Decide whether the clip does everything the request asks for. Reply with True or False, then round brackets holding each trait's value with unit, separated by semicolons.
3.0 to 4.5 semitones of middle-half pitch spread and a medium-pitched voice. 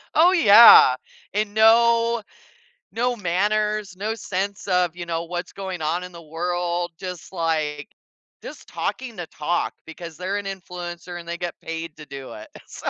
True (3.5 semitones; 180 Hz)